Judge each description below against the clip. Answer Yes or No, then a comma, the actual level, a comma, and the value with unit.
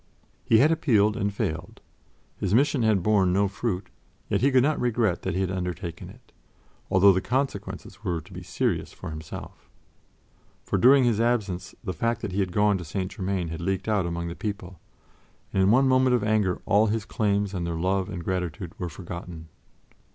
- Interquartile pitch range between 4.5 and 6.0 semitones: No, average, 3.6 semitones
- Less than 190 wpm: No, average, 195 wpm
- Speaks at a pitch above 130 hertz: No, low, 100 Hz